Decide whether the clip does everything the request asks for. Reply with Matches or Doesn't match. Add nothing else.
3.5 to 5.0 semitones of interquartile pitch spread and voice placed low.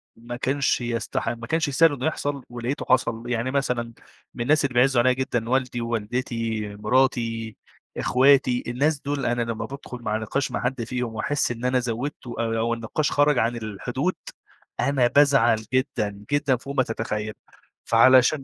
Doesn't match